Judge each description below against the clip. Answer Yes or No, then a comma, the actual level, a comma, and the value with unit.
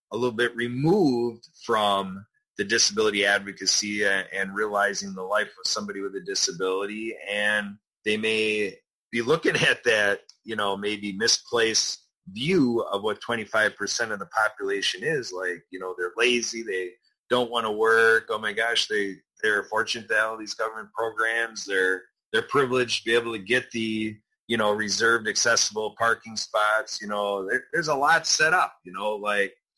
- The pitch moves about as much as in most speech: No, narrow, 2.3 semitones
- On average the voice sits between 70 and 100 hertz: No, low, 110 Hz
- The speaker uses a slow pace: No, average, 165 wpm